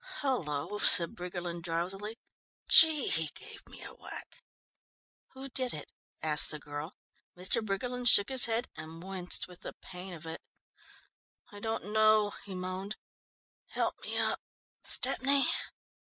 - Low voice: No, high, 190 Hz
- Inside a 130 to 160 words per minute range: Yes, average, 140 wpm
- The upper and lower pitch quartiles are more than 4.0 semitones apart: Yes, average, 4.8 semitones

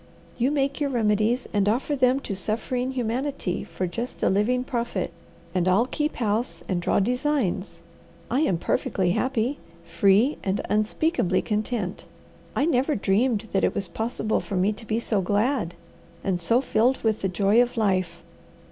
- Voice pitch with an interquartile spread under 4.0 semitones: No, average, 4.6 semitones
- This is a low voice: No, high, 220 Hz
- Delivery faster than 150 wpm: Yes, average, 165 wpm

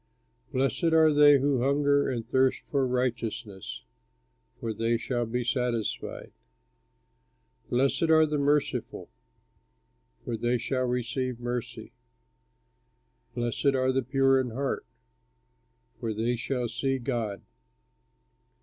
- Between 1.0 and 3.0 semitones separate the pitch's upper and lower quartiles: Yes, narrow, 2.5 semitones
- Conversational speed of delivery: No, slow, 110 wpm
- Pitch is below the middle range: Yes, low, 125 Hz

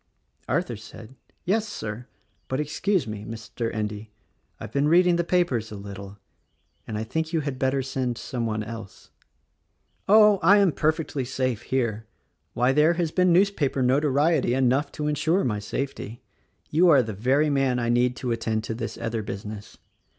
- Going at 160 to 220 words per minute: Yes, average, 170 wpm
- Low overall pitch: Yes, low, 130 Hz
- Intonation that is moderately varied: No, wide, 5.8 semitones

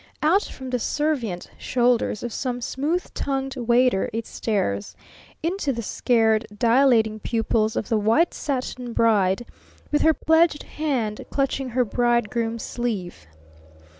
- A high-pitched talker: Yes, high, 240 Hz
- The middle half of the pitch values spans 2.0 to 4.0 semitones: Yes, average, 3.5 semitones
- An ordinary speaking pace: No, slow, 130 wpm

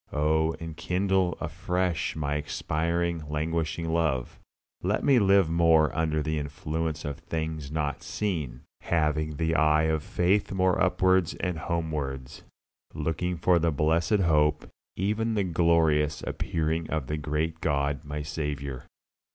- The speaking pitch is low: Yes, very low, 80 Hz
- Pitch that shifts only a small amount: Yes, narrow, 2.3 semitones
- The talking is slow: Yes, slow, 130 wpm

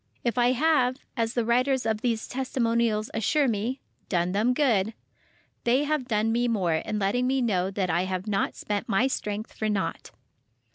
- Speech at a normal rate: Yes, average, 170 wpm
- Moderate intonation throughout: Yes, average, 3.6 semitones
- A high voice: Yes, high, 230 Hz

